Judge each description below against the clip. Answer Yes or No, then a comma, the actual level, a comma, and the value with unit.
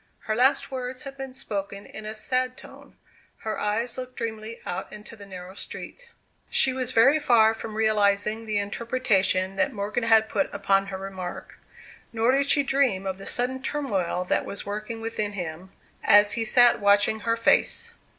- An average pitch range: Yes, average, 3.9 semitones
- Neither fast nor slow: Yes, average, 175 wpm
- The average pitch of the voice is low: No, high, 220 Hz